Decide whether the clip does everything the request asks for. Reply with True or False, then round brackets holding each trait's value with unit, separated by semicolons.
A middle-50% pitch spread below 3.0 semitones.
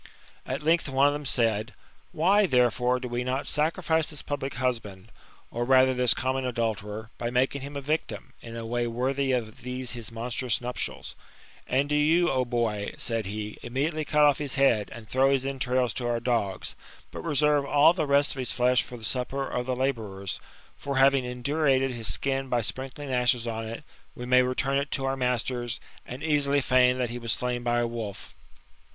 True (2.5 semitones)